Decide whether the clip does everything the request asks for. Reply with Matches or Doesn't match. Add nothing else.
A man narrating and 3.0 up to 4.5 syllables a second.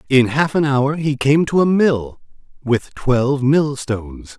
Matches